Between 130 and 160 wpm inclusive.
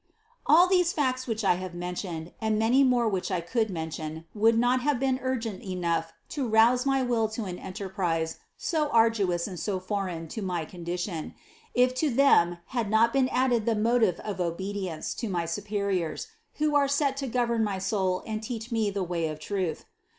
No: average, 185 wpm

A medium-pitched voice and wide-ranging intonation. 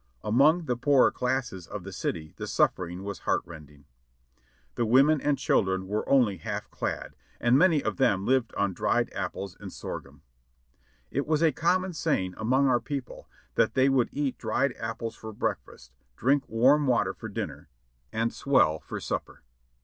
No: low, 120 Hz; wide, 6.1 semitones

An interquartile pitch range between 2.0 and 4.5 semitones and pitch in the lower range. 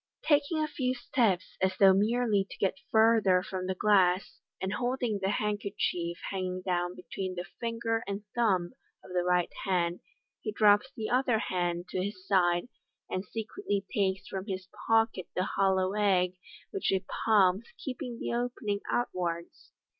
No: average, 3.5 semitones; high, 195 Hz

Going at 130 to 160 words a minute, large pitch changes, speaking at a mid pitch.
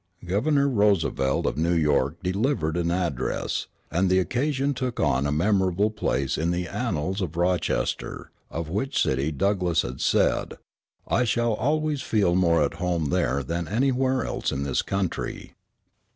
No: average, 150 wpm; wide, 6.0 semitones; very low, 90 Hz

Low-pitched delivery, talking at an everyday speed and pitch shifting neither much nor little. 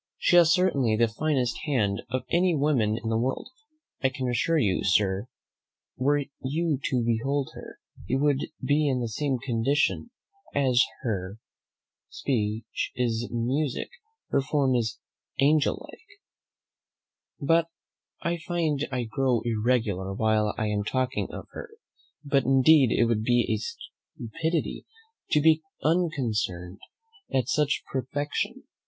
No: low, 130 Hz; slow, 130 wpm; average, 4.5 semitones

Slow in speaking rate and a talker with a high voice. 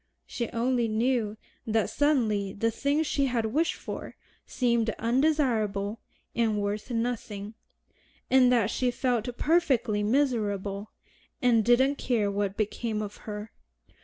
Yes: slow, 125 wpm; high, 230 Hz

